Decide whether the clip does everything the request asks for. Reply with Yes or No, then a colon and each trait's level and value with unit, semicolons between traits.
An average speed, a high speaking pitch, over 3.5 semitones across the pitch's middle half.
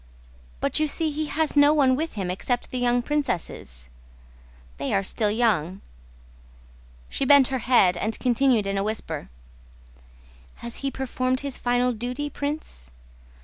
Yes: average, 145 wpm; high, 245 Hz; average, 5.3 semitones